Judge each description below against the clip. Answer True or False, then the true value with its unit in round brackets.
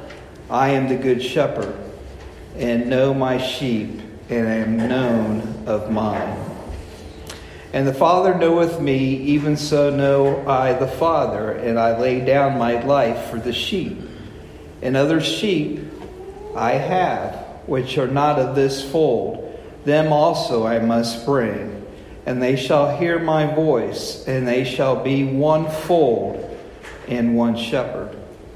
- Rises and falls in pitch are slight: False (4.1 semitones)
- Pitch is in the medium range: False (130 Hz)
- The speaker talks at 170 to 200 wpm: False (135 wpm)